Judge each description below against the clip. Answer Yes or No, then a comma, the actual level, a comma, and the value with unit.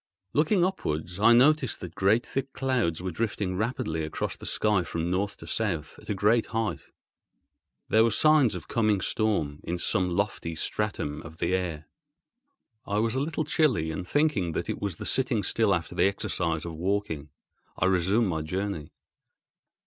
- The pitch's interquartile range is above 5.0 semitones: Yes, wide, 5.4 semitones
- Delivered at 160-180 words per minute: Yes, average, 170 wpm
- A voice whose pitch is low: Yes, low, 100 Hz